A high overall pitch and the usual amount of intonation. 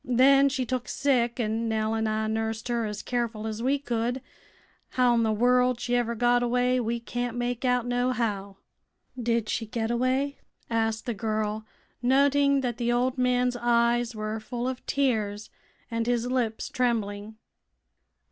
No: high, 240 Hz; narrow, 2.1 semitones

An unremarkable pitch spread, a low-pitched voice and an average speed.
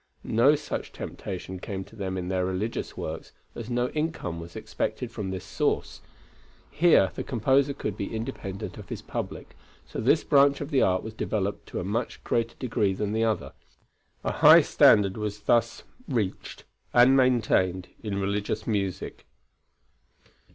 Yes: average, 4.2 semitones; low, 105 Hz; average, 160 wpm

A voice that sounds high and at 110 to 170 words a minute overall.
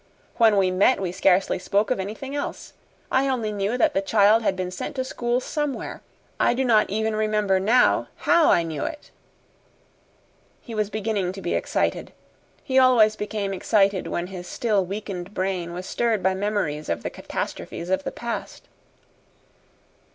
Yes: high, 205 Hz; average, 165 wpm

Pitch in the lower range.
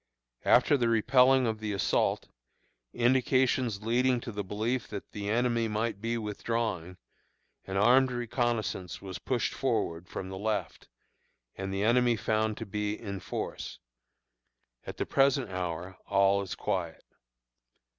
Yes: low, 110 Hz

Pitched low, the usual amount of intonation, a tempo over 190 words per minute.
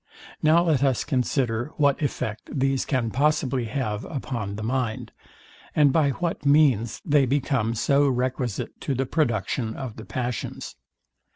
No: low, 130 Hz; average, 3.4 semitones; average, 145 wpm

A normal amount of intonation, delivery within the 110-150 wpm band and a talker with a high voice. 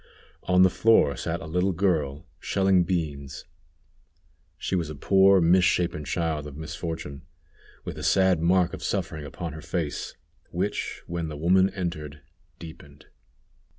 No: average, 3.4 semitones; average, 140 wpm; very low, 85 Hz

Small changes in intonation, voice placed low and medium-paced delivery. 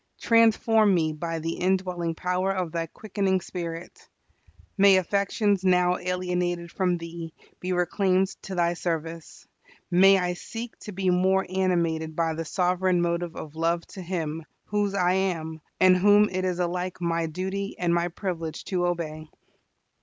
No: narrow, 2.1 semitones; medium, 180 Hz; average, 155 wpm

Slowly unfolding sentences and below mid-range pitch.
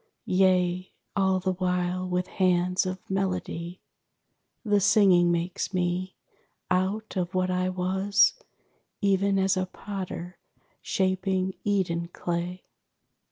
No: slow, 110 wpm; medium, 185 Hz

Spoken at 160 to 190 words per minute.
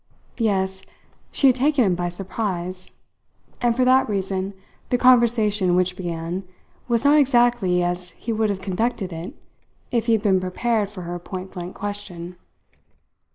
No: average, 150 wpm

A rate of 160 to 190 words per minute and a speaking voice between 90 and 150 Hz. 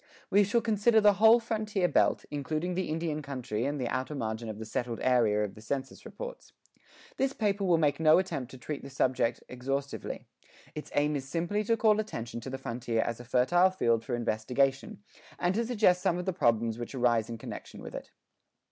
No: average, 200 wpm; medium, 140 Hz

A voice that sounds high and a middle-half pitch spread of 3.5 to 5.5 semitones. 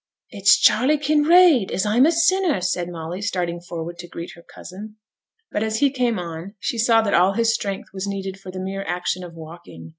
Yes: high, 195 Hz; average, 4.7 semitones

